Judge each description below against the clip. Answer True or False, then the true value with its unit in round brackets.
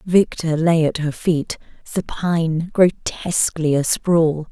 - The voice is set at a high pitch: False (165 Hz)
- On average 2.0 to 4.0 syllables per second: True (3.6 syllables/s)